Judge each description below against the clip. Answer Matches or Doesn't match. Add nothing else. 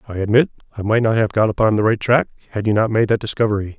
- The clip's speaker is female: Doesn't match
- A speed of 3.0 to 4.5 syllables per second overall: Doesn't match